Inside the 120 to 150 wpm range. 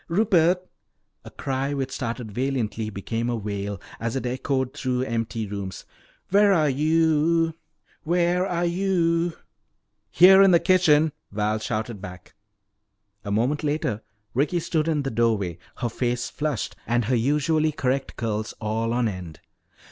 Yes: average, 140 wpm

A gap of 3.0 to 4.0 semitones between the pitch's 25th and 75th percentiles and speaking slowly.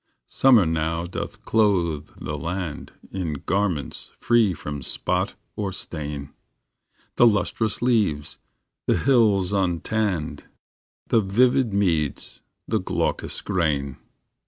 No: wide, 5.5 semitones; slow, 105 wpm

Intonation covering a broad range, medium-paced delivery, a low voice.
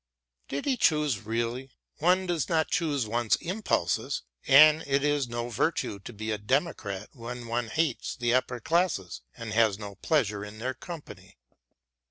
Yes: wide, 5.8 semitones; average, 160 wpm; low, 125 Hz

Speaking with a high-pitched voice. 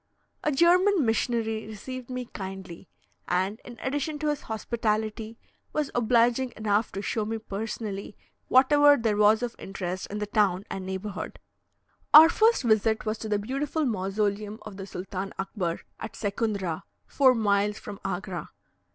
Yes: high, 215 Hz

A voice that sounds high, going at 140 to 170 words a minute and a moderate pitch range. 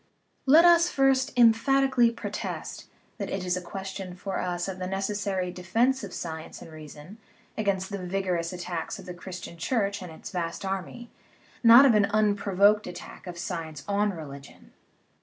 Yes: high, 195 Hz; average, 160 wpm; average, 3.5 semitones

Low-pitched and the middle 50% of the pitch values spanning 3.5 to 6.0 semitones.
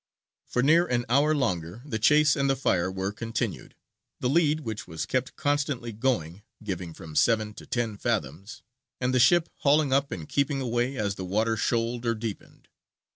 Yes: low, 120 Hz; average, 5.0 semitones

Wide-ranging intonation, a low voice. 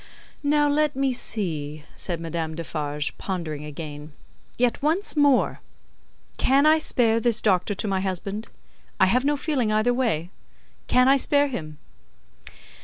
No: wide, 8.7 semitones; high, 215 Hz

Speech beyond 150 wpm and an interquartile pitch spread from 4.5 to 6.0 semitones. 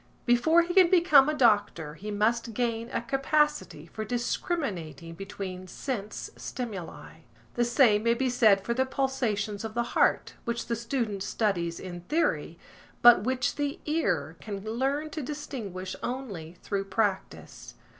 No: average, 145 wpm; average, 5.1 semitones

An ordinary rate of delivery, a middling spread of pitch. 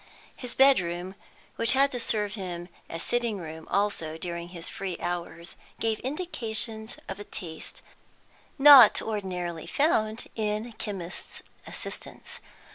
No: slow, 125 wpm; average, 4.9 semitones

